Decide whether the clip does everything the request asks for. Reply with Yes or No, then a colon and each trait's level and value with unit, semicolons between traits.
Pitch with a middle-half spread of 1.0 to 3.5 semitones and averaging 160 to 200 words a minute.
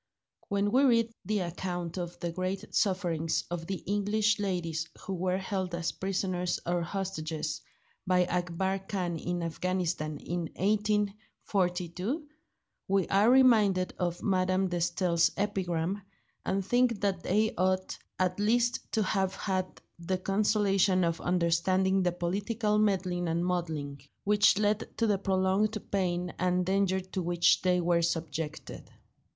No: narrow, 2.4 semitones; slow, 135 wpm